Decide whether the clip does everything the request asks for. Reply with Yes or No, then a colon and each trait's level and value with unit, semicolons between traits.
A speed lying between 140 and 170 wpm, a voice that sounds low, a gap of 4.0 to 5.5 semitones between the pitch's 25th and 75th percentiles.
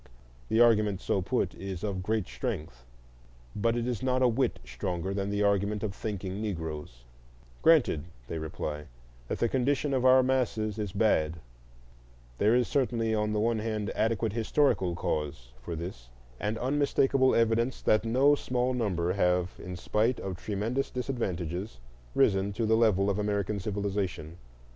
Yes: average, 155 wpm; low, 105 Hz; average, 4.3 semitones